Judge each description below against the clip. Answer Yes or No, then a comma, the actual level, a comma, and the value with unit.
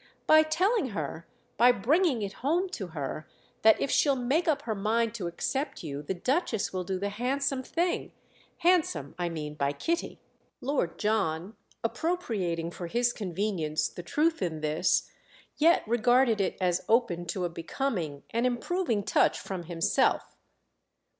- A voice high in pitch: Yes, high, 220 Hz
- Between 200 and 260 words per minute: No, average, 155 wpm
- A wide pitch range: Yes, wide, 7.9 semitones